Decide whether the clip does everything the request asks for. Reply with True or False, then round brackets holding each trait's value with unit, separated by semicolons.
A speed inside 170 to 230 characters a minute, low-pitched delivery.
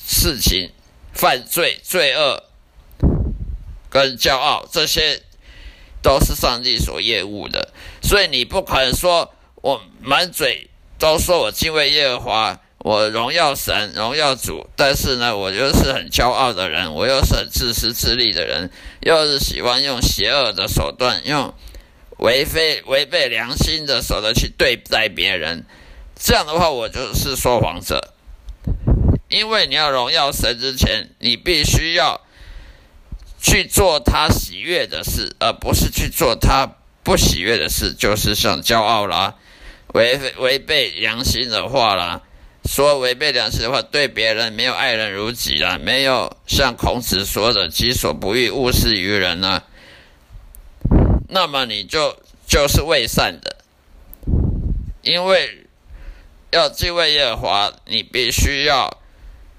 True (200 characters per minute; 105 Hz)